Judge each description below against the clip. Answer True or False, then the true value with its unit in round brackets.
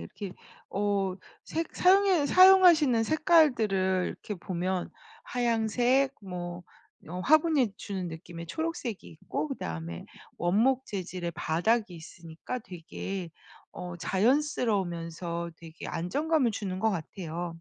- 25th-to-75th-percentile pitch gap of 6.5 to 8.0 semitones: True (7.1 semitones)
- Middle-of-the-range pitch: False (195 Hz)